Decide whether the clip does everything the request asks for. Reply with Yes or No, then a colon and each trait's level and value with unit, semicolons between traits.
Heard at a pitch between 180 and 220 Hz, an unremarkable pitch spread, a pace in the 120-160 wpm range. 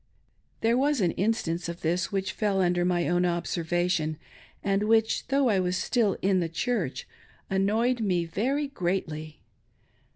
Yes: high, 190 Hz; average, 4.2 semitones; average, 150 wpm